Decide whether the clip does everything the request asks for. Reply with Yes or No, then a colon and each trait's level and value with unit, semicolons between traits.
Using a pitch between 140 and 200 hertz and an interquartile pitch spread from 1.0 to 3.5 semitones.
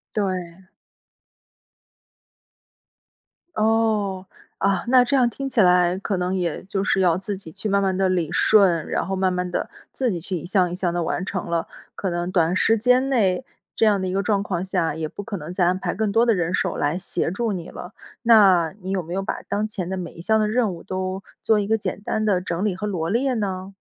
Yes: high, 190 Hz; average, 2.9 semitones